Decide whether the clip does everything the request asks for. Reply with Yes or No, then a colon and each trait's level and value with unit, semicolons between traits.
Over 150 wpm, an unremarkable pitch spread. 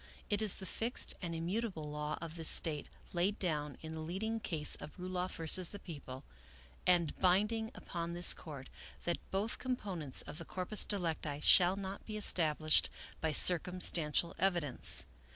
Yes: average, 165 wpm; average, 3.7 semitones